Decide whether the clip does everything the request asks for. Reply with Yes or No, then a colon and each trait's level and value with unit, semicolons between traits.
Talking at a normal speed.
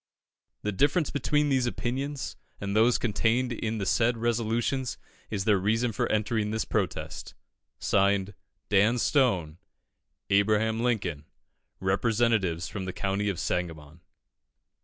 No: slow, 120 wpm